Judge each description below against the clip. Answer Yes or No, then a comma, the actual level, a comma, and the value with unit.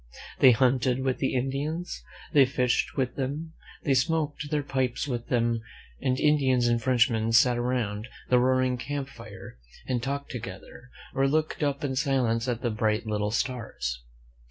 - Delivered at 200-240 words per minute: No, average, 160 wpm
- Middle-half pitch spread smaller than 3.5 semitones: Yes, narrow, 2.6 semitones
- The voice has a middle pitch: No, low, 125 Hz